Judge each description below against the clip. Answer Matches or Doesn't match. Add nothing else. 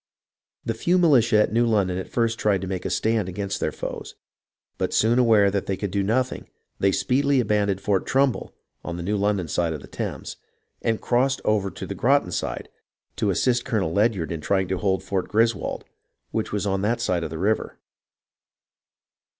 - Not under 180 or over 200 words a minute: Matches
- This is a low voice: Matches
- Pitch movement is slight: Doesn't match